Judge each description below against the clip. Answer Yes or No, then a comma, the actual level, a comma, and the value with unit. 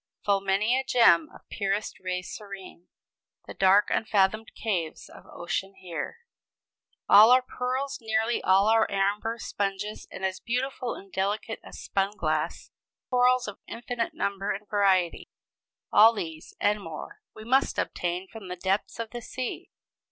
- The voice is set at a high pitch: Yes, high, 205 Hz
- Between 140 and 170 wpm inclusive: Yes, average, 150 wpm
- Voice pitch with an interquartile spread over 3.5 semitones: No, average, 3.1 semitones